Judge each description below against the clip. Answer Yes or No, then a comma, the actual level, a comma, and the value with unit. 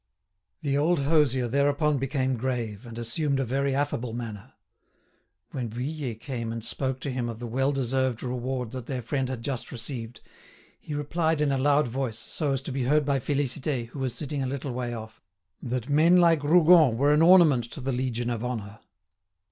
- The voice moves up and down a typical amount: Yes, average, 3.2 semitones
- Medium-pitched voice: No, low, 130 Hz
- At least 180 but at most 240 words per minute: Yes, average, 190 wpm